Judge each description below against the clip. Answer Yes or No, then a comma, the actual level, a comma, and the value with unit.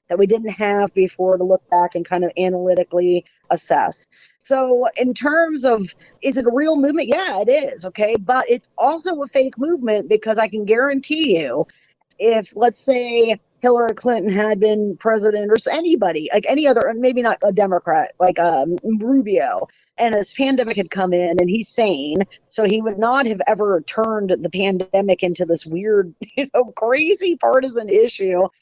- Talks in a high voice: Yes, high, 220 Hz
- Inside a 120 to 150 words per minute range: No, average, 175 wpm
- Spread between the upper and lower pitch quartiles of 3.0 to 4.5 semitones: No, wide, 5.4 semitones